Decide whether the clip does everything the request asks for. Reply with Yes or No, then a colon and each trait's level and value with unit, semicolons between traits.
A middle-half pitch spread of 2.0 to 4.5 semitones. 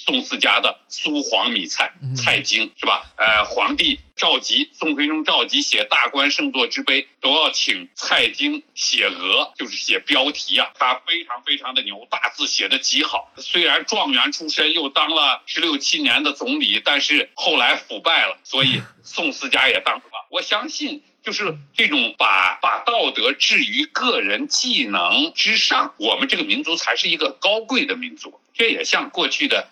No: average, 5.3 semitones